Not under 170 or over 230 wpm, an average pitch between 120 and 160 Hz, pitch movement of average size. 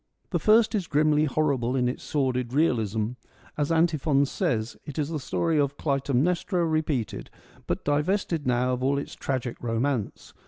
No: average, 155 wpm; medium, 140 Hz; average, 3.7 semitones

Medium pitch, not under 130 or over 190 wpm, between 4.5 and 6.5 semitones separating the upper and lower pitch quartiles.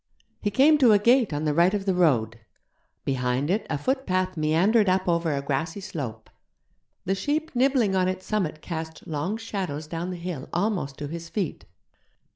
Yes: medium, 180 Hz; average, 180 wpm; average, 5.2 semitones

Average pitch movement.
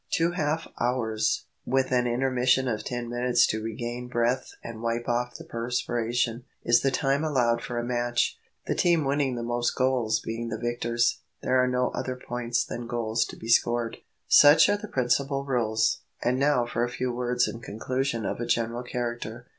No: narrow, 1.5 semitones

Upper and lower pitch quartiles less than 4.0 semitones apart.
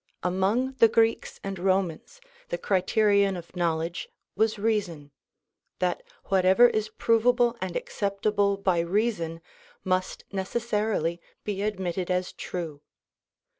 Yes: average, 3.4 semitones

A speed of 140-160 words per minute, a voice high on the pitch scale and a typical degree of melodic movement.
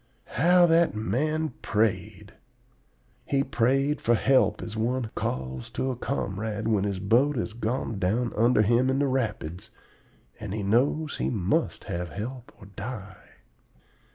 No: average, 145 wpm; low, 115 Hz; average, 4.3 semitones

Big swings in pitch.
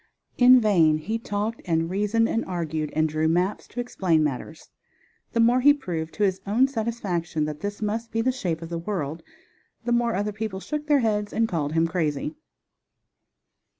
Yes: wide, 5.9 semitones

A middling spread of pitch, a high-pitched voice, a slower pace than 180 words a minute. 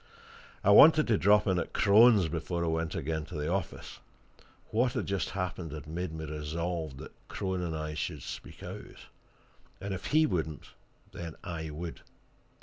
No: average, 3.7 semitones; very low, 85 Hz; average, 170 wpm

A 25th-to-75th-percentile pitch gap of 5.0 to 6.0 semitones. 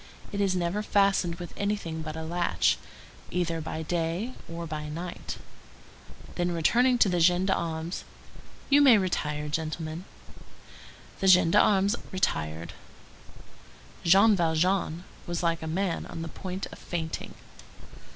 No: average, 3.1 semitones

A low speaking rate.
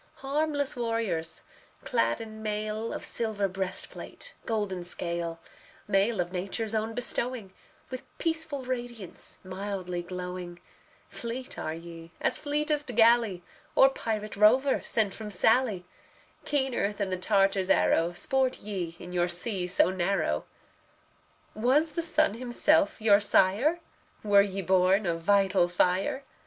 Yes: slow, 125 wpm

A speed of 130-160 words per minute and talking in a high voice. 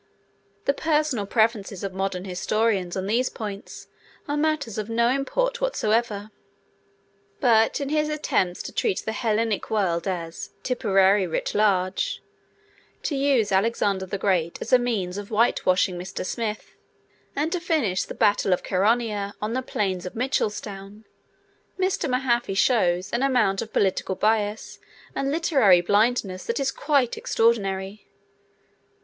Yes: average, 140 wpm; high, 215 Hz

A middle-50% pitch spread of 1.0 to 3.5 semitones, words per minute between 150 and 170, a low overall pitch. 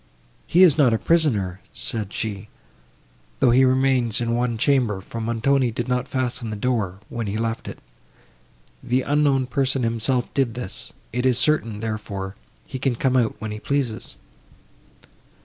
Yes: average, 3.1 semitones; average, 160 wpm; low, 120 Hz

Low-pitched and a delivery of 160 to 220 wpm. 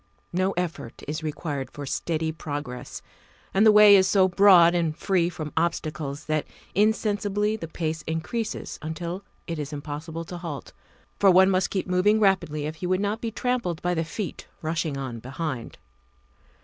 No: medium, 170 Hz; average, 165 wpm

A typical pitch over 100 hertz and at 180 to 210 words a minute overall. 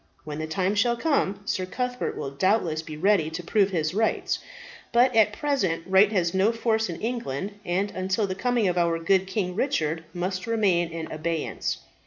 Yes: high, 190 Hz; average, 185 wpm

